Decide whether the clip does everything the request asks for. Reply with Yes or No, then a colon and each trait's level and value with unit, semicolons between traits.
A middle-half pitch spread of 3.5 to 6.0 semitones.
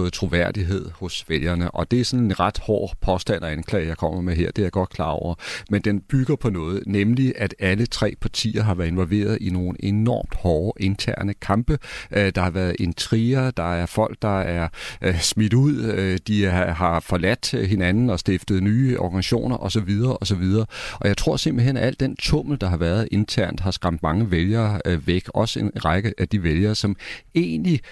Yes: average, 3.9 semitones